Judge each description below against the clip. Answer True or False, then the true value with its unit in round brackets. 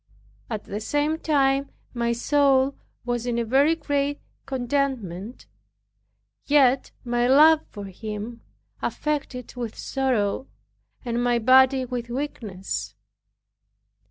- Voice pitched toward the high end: True (250 Hz)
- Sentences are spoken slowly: True (110 wpm)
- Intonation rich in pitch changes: False (3.0 semitones)